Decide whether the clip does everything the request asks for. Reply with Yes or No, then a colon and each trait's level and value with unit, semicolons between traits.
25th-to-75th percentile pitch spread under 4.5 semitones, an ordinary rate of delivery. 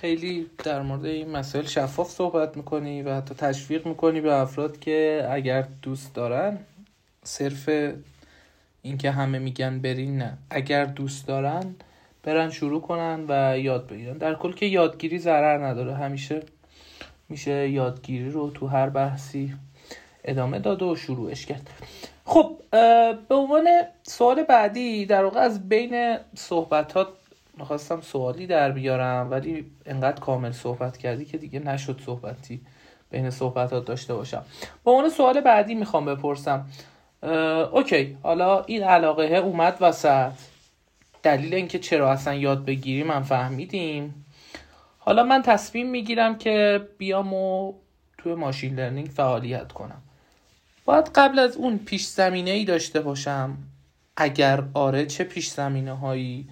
No: average, 5.2 semitones; average, 135 wpm